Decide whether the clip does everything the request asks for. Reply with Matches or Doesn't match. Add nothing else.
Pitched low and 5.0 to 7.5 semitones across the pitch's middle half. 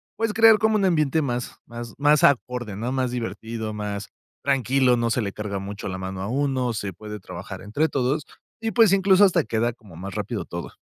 Matches